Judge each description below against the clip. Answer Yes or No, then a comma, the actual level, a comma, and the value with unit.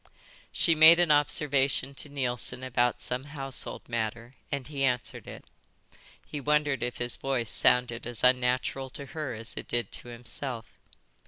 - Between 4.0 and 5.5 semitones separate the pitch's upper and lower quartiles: No, average, 2.8 semitones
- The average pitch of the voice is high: No, low, 130 Hz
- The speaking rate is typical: Yes, average, 150 wpm